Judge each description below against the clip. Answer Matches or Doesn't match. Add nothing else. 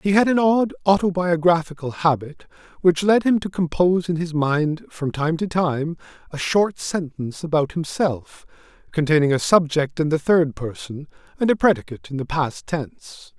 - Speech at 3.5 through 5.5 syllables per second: Matches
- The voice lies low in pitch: Doesn't match